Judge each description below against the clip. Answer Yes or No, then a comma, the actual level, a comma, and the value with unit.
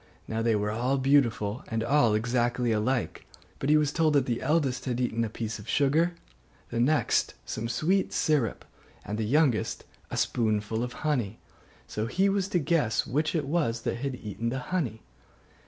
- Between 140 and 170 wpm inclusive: No, average, 180 wpm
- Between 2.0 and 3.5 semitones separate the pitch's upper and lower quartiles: No, average, 4.7 semitones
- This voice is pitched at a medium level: No, low, 125 Hz